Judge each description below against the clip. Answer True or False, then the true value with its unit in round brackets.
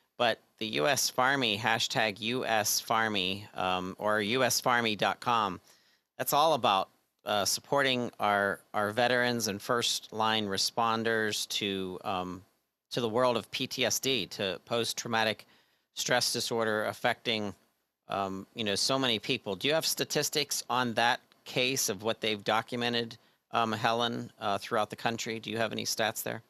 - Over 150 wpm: False (145 wpm)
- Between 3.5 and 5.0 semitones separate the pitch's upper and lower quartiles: False (2.8 semitones)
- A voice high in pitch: False (115 Hz)